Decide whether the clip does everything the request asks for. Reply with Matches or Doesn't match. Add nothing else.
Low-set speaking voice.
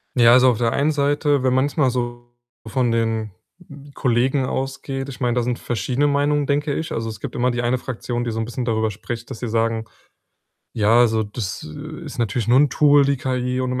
Matches